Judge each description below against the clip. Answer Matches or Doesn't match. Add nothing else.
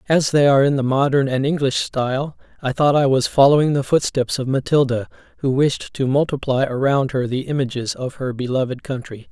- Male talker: Matches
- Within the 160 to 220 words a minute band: Matches